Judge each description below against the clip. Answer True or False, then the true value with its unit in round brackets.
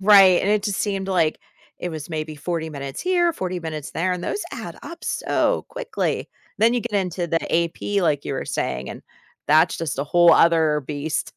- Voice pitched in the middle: True (170 Hz)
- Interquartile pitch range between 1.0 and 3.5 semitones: False (4.1 semitones)